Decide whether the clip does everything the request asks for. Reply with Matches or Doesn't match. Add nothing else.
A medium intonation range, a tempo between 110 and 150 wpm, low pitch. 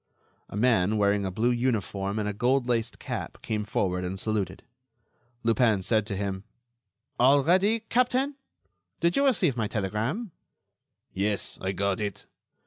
Matches